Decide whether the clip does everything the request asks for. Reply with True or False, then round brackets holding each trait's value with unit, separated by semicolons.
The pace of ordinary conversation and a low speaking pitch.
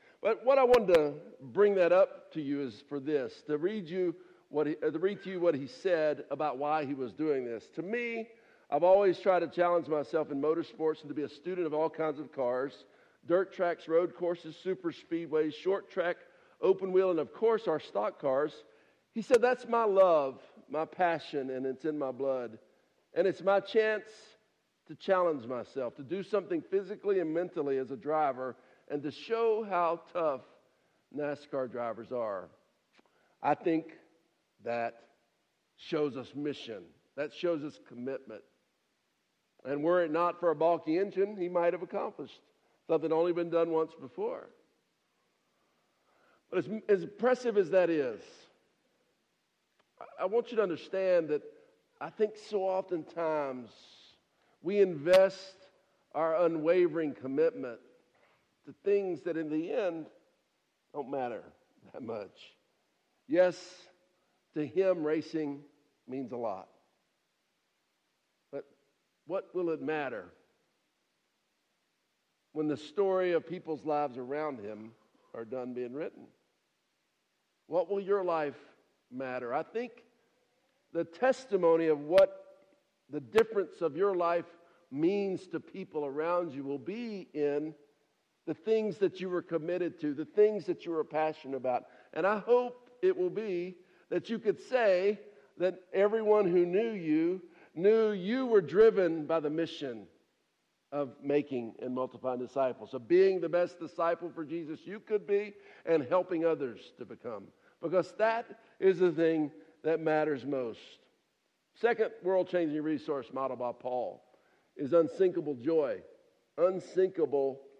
False (145 wpm; 170 Hz)